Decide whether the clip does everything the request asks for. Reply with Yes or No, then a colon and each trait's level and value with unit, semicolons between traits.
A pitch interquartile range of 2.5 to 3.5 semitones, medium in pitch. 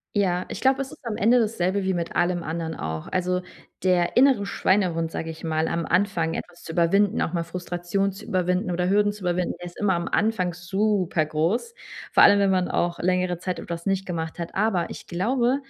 Yes: average, 2.9 semitones; medium, 180 Hz